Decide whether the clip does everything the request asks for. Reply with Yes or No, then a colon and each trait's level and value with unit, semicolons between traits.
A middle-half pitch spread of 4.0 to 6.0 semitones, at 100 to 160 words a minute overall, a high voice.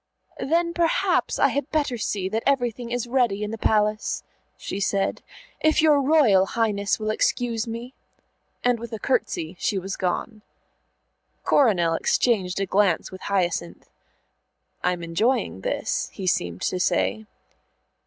Yes: average, 4.5 semitones; average, 140 wpm; high, 215 Hz